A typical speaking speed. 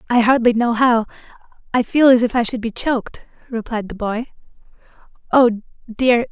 Yes: average, 160 wpm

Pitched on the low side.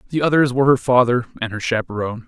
Yes: low, 125 Hz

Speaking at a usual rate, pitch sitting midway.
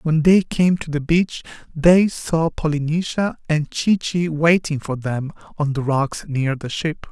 Yes: average, 175 wpm; medium, 155 Hz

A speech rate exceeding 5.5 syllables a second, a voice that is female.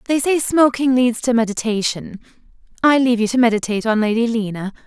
Yes: 6.0 syllables/s; female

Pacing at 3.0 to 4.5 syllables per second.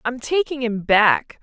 Yes: 3.8 syllables/s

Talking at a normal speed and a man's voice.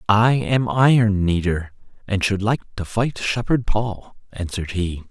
Yes: average, 155 wpm; male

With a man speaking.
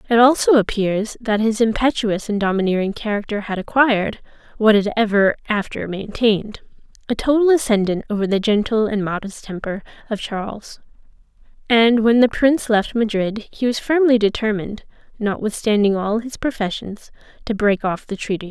No: female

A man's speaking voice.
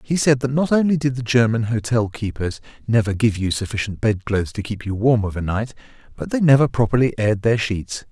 Yes: male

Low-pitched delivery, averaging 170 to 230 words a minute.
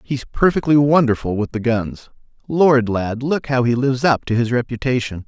Yes: low, 125 Hz; average, 180 wpm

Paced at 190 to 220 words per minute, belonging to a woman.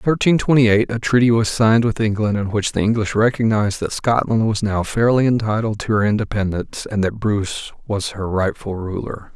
No: average, 200 wpm; male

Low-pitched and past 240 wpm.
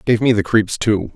Yes: low, 105 Hz; fast, 260 wpm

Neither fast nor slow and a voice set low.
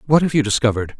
No: fast, 240 wpm; low, 125 Hz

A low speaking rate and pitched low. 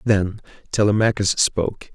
Yes: slow, 90 wpm; low, 100 Hz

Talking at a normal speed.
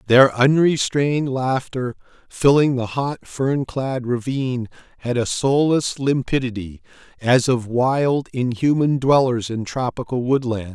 No: slow, 115 wpm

